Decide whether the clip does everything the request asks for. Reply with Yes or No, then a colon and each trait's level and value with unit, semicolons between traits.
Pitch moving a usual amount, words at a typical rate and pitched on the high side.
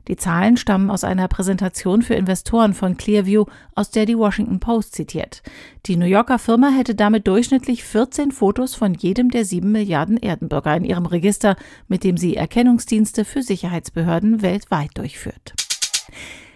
Yes: average, 3.7 semitones; average, 150 wpm; high, 205 Hz